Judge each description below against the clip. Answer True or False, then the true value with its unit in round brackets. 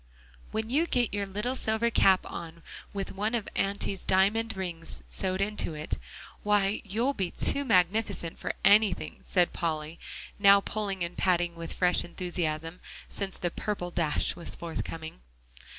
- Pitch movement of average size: True (3.5 semitones)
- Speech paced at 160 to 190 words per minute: False (150 wpm)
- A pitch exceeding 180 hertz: True (190 Hz)